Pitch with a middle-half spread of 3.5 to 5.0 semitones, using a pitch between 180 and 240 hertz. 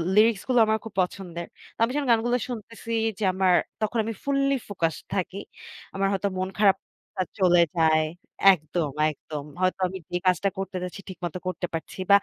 Yes: average, 3.8 semitones; high, 190 Hz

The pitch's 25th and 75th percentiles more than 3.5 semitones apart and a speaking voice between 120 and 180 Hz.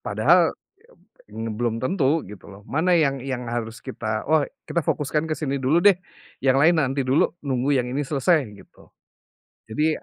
Yes: average, 4.1 semitones; low, 135 Hz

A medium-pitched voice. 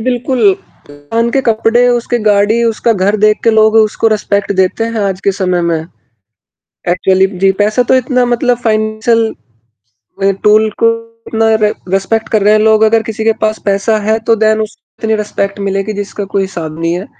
No: high, 215 Hz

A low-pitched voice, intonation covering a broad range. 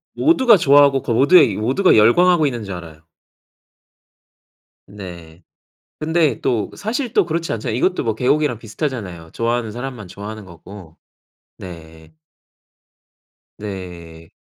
Yes: low, 115 Hz; wide, 8.4 semitones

